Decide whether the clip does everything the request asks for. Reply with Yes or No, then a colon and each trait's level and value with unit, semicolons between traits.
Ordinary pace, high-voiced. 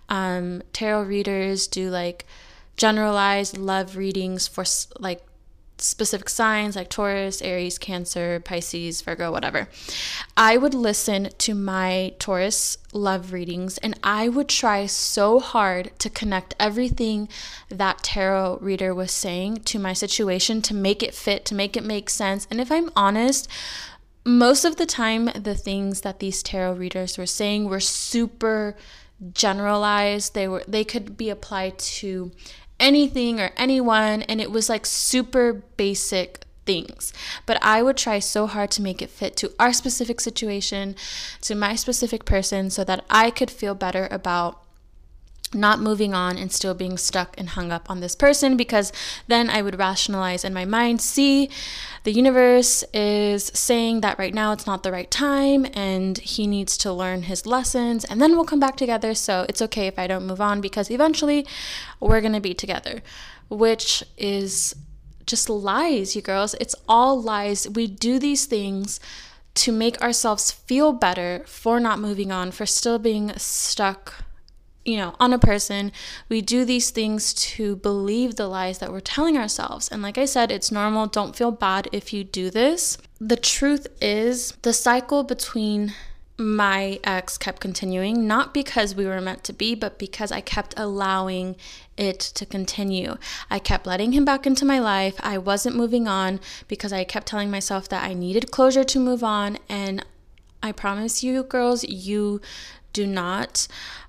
Yes: average, 165 wpm; high, 210 Hz